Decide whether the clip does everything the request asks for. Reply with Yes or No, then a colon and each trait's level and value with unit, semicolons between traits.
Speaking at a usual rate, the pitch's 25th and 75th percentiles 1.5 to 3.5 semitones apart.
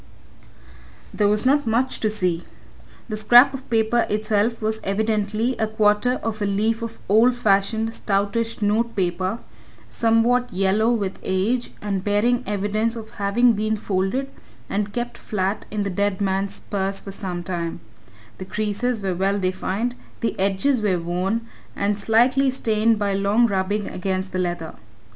Yes: average, 150 wpm; average, 2.8 semitones